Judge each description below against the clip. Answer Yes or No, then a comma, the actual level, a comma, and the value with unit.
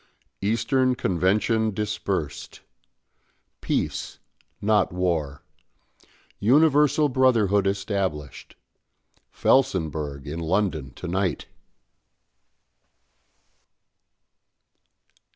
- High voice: No, low, 100 Hz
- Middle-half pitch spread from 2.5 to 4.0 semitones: No, wide, 5.4 semitones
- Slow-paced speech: Yes, slow, 55 wpm